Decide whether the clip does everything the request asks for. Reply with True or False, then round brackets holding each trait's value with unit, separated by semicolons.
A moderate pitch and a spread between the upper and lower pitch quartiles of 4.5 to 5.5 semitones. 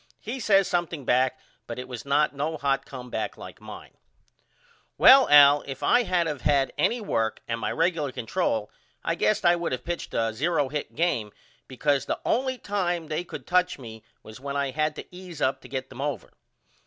True (145 Hz; 5.1 semitones)